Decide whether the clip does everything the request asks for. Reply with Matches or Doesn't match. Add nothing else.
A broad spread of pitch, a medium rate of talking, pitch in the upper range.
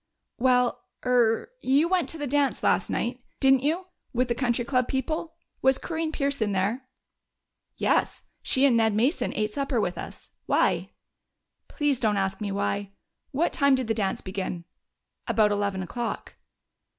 Doesn't match